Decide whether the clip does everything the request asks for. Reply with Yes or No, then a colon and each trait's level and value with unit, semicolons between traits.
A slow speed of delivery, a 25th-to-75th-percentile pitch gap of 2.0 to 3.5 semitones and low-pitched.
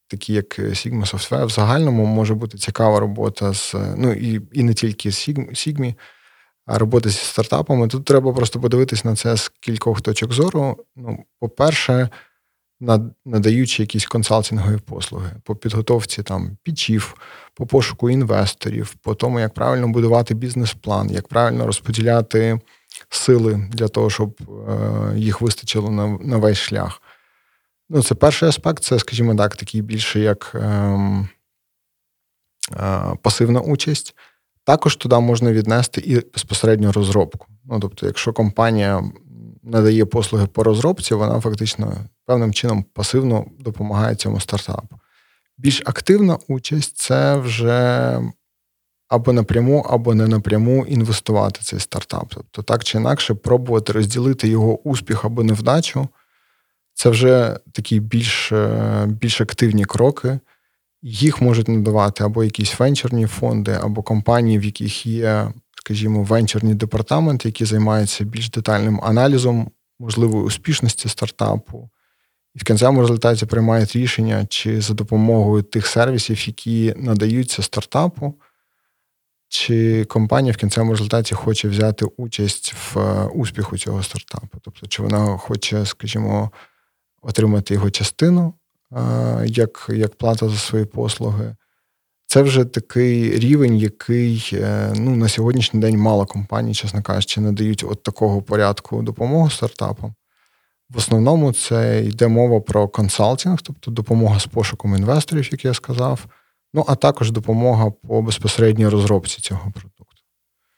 No: average, 125 wpm; narrow, 2.4 semitones; low, 110 Hz